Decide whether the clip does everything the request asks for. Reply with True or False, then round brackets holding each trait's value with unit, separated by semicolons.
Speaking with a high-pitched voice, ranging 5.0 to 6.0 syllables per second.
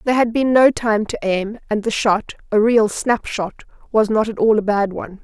True (215 Hz; 5.2 syllables/s)